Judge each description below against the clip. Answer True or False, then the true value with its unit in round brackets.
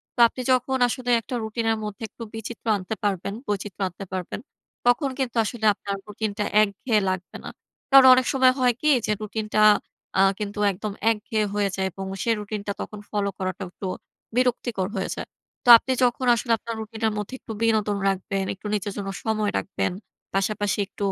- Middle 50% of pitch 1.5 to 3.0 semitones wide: True (2.7 semitones)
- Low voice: False (215 Hz)